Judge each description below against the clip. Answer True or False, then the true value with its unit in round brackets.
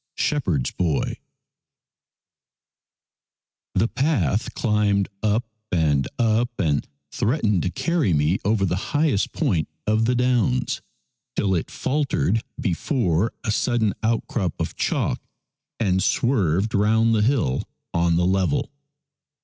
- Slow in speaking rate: True (115 wpm)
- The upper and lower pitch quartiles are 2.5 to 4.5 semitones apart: False (5.1 semitones)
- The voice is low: True (105 Hz)